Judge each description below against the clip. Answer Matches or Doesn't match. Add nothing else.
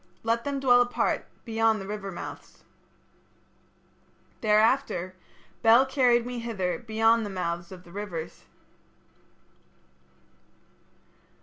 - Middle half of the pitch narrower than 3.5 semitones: Doesn't match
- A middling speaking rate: Doesn't match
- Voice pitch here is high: Matches